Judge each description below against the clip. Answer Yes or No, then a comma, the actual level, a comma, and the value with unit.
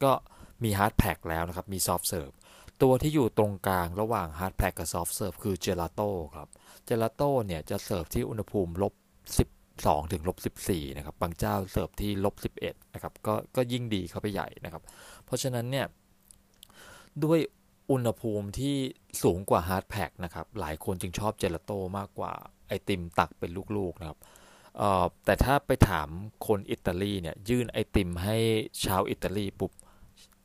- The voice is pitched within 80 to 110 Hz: Yes, low, 100 Hz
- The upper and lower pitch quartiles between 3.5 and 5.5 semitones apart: No, average, 3.1 semitones